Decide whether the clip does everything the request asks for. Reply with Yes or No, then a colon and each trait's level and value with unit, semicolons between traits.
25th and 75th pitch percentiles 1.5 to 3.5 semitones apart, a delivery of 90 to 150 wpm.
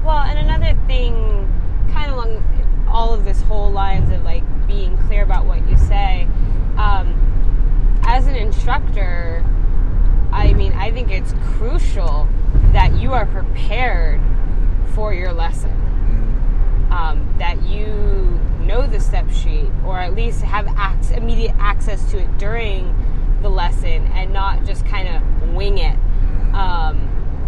Yes: narrow, 2.6 semitones; average, 140 wpm